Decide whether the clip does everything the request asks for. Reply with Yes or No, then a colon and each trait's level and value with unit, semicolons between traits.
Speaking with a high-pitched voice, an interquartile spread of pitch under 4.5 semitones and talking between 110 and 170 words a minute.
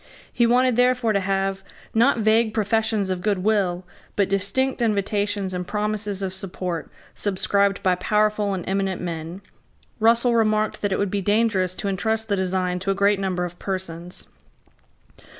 Yes: high, 200 Hz; narrow, 2.5 semitones; average, 160 wpm